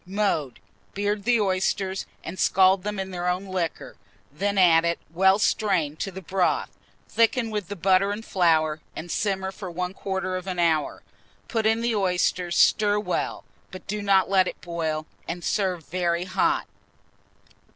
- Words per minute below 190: Yes, average, 160 wpm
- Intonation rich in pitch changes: No, narrow, 2.5 semitones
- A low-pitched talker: No, high, 190 Hz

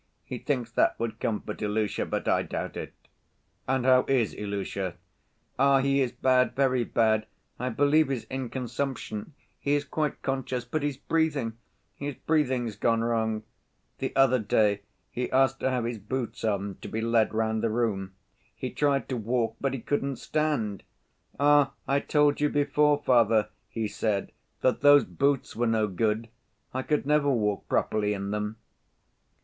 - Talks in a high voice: No, low, 125 Hz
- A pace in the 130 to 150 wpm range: No, average, 165 wpm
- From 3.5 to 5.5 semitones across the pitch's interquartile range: Yes, average, 4.0 semitones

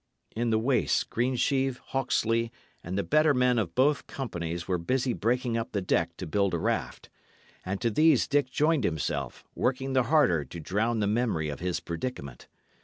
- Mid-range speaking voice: No, low, 115 Hz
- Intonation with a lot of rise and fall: Yes, wide, 6.8 semitones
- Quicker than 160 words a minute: Yes, average, 180 wpm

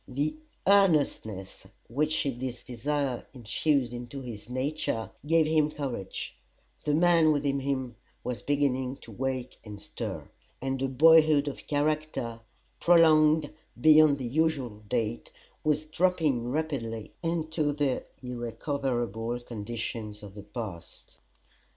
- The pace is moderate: No, slow, 115 wpm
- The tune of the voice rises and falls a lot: No, average, 4.5 semitones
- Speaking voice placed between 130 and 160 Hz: Yes, low, 135 Hz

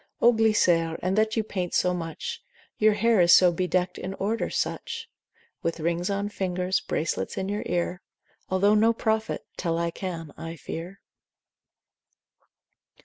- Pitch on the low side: No, medium, 185 Hz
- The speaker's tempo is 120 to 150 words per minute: Yes, average, 145 wpm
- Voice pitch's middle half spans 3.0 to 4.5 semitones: Yes, average, 3.6 semitones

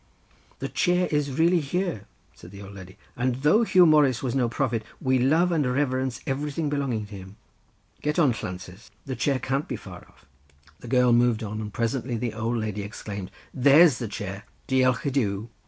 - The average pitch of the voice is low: Yes, low, 125 Hz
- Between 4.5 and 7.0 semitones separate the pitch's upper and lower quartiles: Yes, average, 4.8 semitones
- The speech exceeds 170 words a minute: Yes, average, 190 wpm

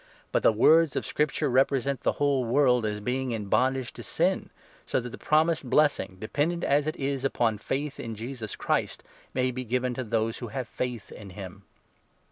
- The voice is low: Yes, low, 125 Hz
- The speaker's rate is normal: Yes, average, 195 wpm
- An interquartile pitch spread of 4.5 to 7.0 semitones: No, average, 3.5 semitones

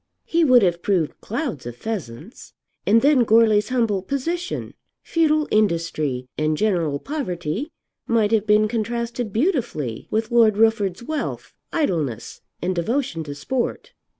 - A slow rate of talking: Yes, slow, 130 wpm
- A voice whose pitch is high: Yes, high, 215 Hz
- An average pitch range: No, wide, 6.3 semitones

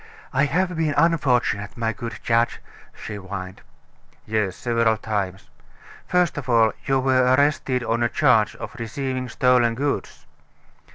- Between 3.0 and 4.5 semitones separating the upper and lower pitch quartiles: Yes, average, 3.5 semitones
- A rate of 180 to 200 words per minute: No, slow, 135 wpm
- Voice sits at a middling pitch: No, low, 120 Hz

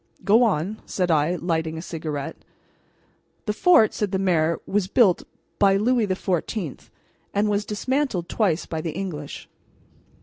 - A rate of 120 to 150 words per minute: Yes, average, 140 wpm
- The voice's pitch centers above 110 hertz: Yes, high, 190 Hz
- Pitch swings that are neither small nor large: Yes, average, 4.5 semitones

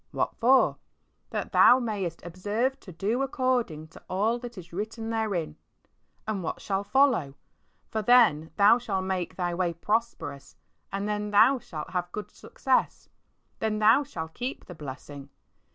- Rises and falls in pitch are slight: No, average, 5.1 semitones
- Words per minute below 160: Yes, average, 150 wpm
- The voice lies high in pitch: Yes, high, 205 Hz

